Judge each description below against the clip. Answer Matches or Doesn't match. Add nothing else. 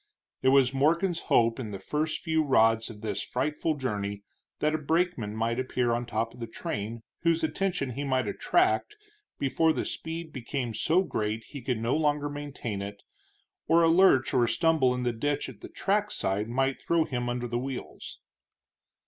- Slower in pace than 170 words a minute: Doesn't match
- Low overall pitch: Matches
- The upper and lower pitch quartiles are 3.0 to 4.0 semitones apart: Doesn't match